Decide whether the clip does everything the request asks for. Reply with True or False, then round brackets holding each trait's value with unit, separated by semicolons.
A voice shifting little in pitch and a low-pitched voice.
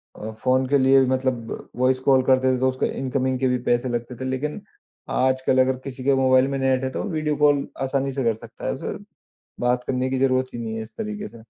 True (1.0 semitones; 130 Hz)